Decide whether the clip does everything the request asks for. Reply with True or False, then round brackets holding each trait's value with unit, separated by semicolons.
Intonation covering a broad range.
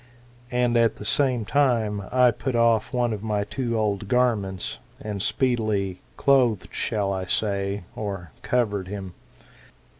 False (3.6 semitones)